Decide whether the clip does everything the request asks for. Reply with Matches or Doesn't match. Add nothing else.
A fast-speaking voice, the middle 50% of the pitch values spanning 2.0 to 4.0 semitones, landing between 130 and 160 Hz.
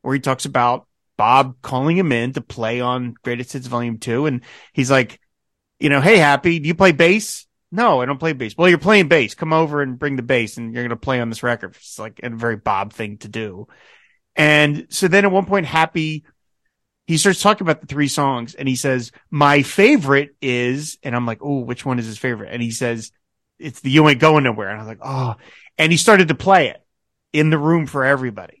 Doesn't match